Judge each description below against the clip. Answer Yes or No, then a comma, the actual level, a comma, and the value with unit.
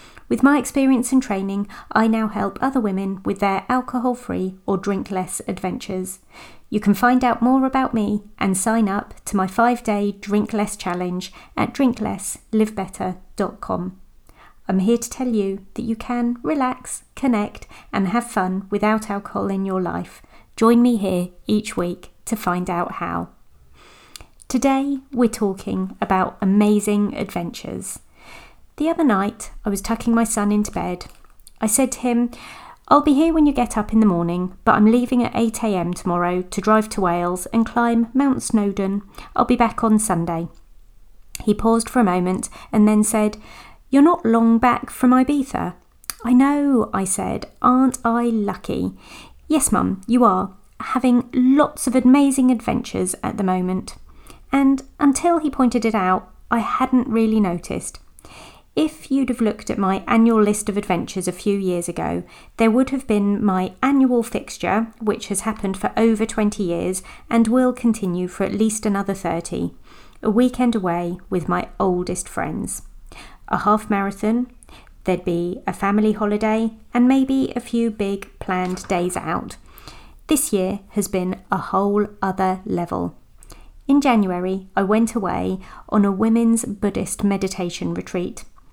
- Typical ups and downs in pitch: Yes, average, 4.2 semitones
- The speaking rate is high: No, average, 160 wpm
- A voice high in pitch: Yes, high, 215 Hz